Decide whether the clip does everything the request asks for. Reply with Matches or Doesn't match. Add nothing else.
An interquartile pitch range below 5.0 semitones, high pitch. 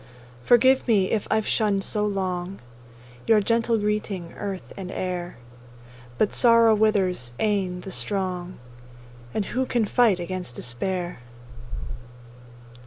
Matches